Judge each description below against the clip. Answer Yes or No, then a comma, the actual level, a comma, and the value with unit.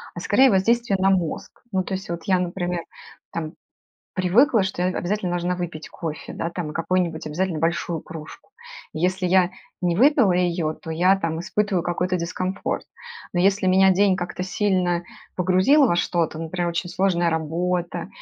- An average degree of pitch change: No, narrow, 1.9 semitones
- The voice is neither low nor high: Yes, medium, 180 Hz